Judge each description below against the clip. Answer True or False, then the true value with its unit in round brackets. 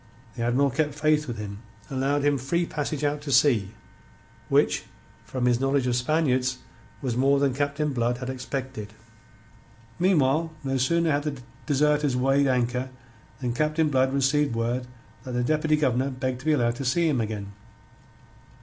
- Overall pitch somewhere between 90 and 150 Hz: True (135 Hz)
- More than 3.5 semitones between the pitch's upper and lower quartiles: False (2.9 semitones)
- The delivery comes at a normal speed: True (165 wpm)